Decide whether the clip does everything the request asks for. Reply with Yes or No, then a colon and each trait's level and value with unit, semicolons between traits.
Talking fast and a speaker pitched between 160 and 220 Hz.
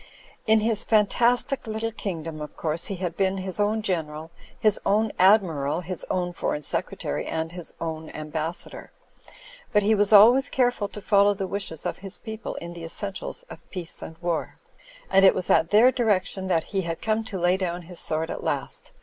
No: average, 195 wpm; high, 190 Hz